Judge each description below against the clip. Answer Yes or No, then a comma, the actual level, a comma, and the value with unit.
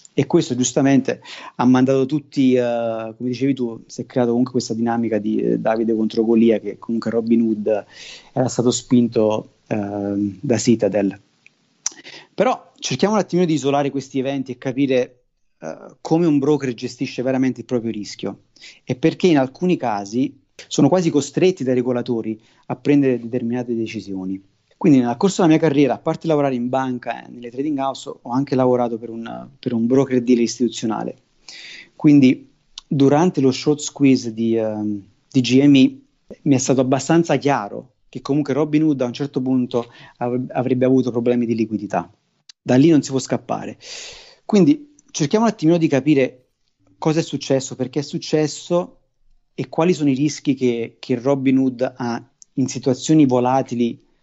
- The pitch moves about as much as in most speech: Yes, average, 3.2 semitones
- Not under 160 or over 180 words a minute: Yes, average, 165 wpm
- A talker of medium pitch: No, low, 130 Hz